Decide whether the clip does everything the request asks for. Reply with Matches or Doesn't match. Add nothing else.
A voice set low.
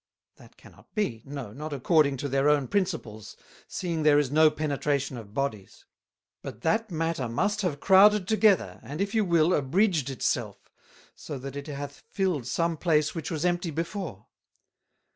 Doesn't match